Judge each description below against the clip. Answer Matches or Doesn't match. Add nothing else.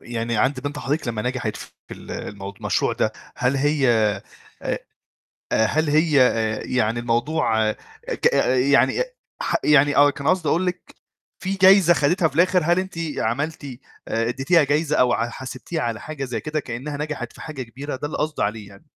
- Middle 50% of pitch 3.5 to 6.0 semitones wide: Matches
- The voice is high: Doesn't match